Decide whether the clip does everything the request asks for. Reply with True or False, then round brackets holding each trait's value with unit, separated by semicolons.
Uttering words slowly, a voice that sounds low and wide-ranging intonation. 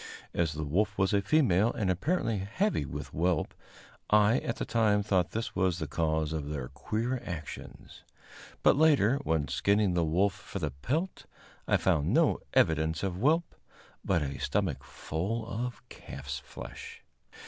False (160 wpm; 95 Hz; 6.2 semitones)